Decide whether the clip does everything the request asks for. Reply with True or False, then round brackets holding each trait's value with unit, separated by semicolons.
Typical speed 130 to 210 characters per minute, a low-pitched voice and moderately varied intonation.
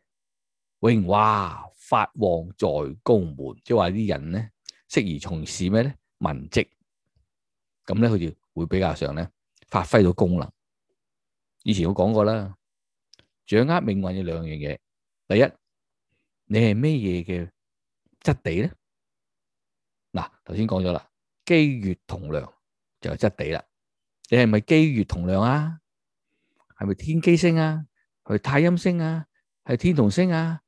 False (190 characters per minute; 105 Hz; 8.0 semitones)